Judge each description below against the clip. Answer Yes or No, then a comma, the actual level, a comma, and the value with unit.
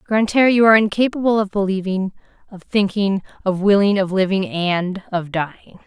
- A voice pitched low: No, high, 200 Hz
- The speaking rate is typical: Yes, average, 155 wpm